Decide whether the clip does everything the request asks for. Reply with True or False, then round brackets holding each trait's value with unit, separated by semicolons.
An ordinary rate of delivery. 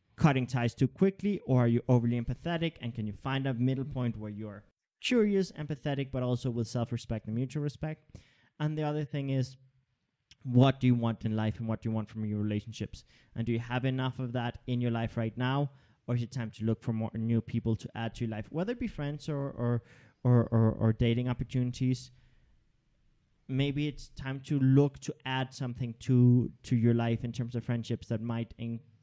False (215 wpm)